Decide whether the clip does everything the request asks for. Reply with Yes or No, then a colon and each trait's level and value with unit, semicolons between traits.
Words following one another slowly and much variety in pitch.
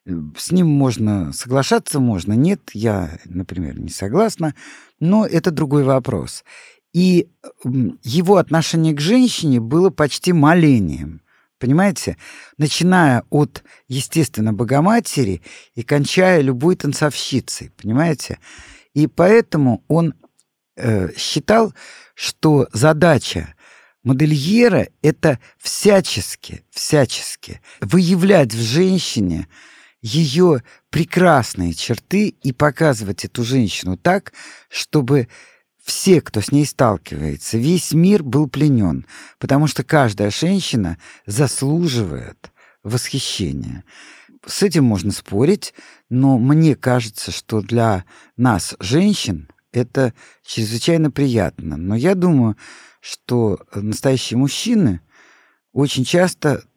Yes: slow, 95 wpm; wide, 6.5 semitones